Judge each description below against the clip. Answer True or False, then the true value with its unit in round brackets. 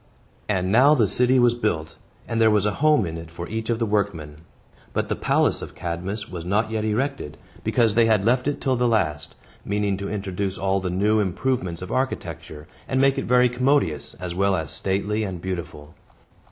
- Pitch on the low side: True (100 Hz)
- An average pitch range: True (4.7 semitones)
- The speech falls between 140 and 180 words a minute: False (200 wpm)